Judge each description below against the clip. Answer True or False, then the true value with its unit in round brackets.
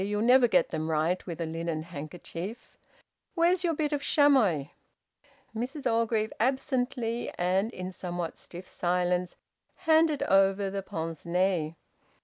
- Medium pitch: False (195 Hz)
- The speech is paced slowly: True (130 wpm)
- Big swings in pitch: True (6.2 semitones)